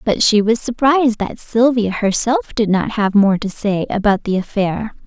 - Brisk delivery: No, average, 190 wpm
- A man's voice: No, female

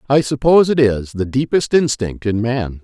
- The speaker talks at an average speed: Yes, average, 190 wpm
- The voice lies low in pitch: Yes, low, 125 Hz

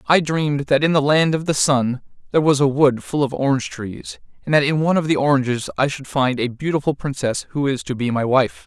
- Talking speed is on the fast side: Yes, fast, 250 wpm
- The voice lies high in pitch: No, medium, 140 Hz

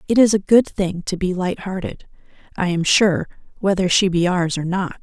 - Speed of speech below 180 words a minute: No, fast, 205 wpm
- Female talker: Yes, female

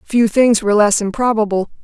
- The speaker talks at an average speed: Yes, average, 165 wpm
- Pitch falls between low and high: No, high, 215 Hz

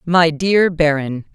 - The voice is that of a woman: Yes, female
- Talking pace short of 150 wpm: Yes, slow, 135 wpm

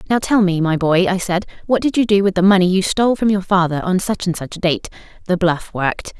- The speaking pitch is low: No, high, 190 Hz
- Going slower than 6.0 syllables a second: No, 6.1 syllables/s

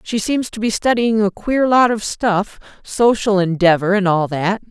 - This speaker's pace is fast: No, average, 180 wpm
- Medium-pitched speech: No, high, 210 Hz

